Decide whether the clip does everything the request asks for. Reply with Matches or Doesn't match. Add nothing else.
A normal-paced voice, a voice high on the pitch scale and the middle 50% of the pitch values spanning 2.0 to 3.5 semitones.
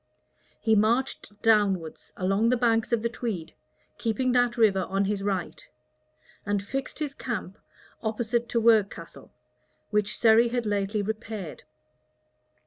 Doesn't match